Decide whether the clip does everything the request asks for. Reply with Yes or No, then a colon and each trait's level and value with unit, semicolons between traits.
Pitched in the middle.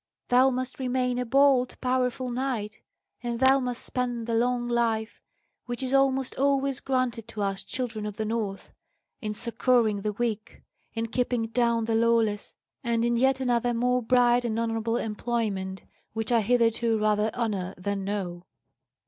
No: high, 235 Hz